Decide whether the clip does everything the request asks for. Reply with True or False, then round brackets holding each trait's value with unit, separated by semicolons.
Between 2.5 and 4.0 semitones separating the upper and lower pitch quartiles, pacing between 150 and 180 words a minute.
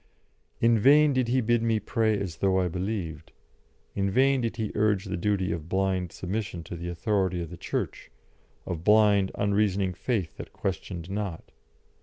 True (3.4 semitones; 170 wpm)